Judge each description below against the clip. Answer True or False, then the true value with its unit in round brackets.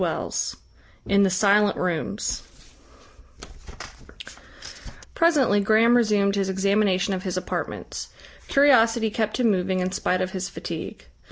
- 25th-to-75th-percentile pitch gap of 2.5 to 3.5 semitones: True (2.9 semitones)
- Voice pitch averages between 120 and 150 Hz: False (200 Hz)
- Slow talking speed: True (120 wpm)